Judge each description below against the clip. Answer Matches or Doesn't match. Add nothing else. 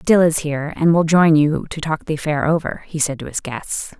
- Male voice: Doesn't match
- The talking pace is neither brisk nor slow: Doesn't match